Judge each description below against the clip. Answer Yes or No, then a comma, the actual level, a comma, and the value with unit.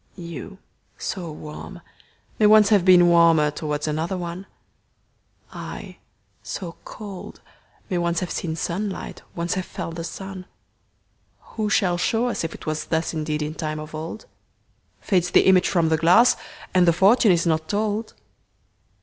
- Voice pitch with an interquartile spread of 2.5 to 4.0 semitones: Yes, average, 3.4 semitones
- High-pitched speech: No, medium, 175 Hz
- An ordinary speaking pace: No, slow, 130 wpm